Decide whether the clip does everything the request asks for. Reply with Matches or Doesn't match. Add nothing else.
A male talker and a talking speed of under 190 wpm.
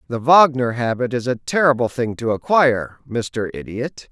Matches